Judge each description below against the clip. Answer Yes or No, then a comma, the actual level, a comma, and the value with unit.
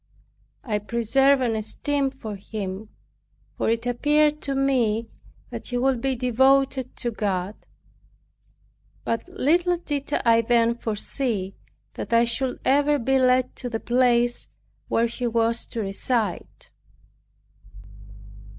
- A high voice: Yes, high, 240 Hz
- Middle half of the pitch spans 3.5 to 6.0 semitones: No, average, 3.1 semitones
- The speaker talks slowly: Yes, slow, 125 wpm